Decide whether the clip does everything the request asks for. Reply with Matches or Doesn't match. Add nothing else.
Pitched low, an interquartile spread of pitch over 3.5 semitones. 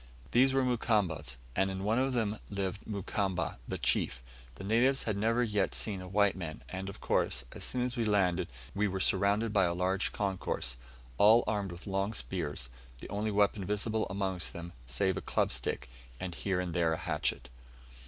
Doesn't match